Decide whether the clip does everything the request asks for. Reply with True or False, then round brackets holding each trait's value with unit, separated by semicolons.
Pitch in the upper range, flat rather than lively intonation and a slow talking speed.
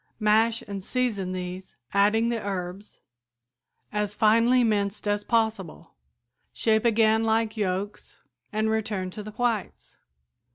True (215 Hz; 2.0 semitones; 120 wpm)